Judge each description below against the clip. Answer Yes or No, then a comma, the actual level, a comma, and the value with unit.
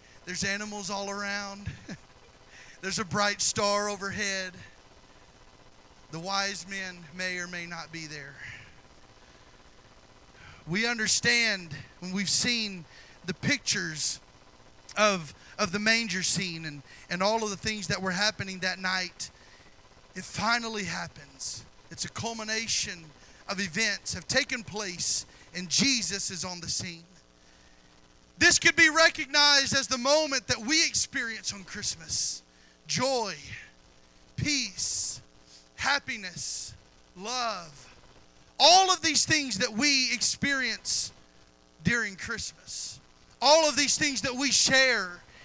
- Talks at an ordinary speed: No, slow, 120 wpm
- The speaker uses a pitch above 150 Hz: Yes, high, 190 Hz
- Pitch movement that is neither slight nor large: No, wide, 9.0 semitones